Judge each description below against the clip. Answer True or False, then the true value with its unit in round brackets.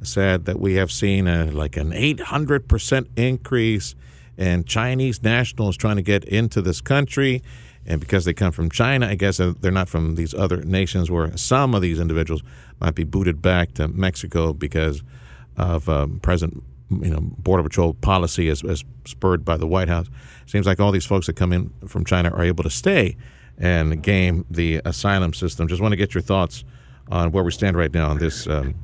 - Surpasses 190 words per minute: True (200 wpm)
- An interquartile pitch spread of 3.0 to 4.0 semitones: True (3.5 semitones)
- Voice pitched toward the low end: True (90 Hz)